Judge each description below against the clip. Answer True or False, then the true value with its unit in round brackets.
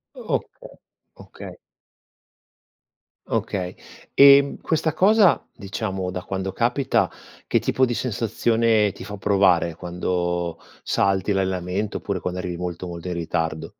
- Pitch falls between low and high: False (95 Hz)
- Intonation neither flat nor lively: True (4.3 semitones)